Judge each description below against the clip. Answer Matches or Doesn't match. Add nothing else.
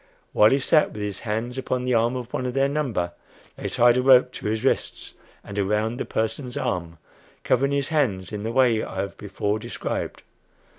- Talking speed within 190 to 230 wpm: Matches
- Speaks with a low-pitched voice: Matches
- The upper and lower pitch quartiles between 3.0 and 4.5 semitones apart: Matches